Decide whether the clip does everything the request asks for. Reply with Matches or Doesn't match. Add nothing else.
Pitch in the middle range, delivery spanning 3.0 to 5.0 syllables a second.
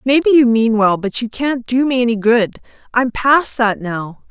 Doesn't match